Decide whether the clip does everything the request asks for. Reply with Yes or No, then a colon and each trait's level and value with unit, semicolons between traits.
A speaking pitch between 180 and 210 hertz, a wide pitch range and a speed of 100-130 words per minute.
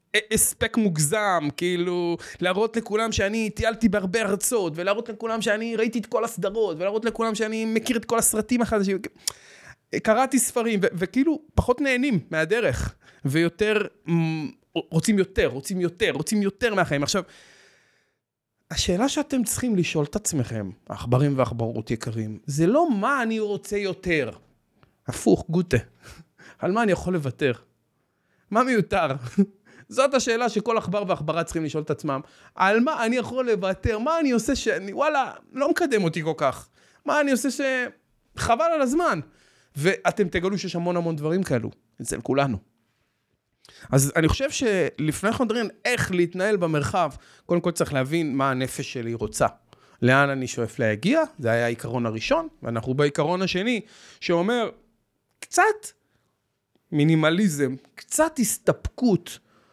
No: high, 190 Hz; wide, 7.2 semitones; average, 140 wpm